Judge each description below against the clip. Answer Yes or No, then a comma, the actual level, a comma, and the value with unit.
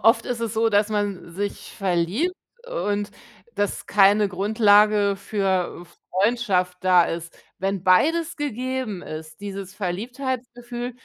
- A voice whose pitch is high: Yes, high, 205 Hz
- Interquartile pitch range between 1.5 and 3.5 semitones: No, average, 4.0 semitones